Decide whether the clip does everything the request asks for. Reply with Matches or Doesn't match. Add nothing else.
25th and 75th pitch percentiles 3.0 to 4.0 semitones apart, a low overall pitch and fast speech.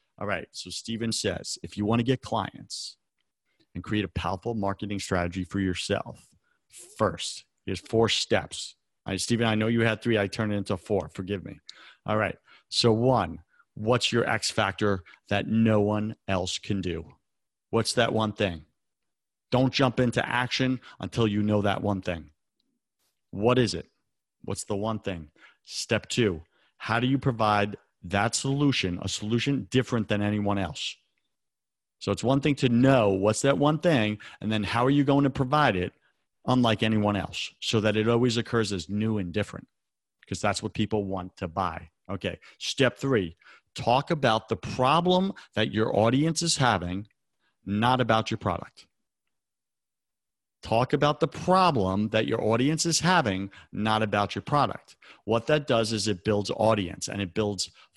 Doesn't match